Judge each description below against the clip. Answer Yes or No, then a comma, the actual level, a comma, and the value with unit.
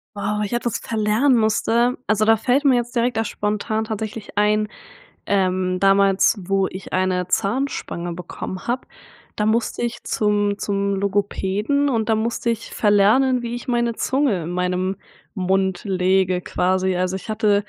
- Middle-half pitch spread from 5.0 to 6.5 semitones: No, average, 3.4 semitones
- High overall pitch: Yes, high, 210 Hz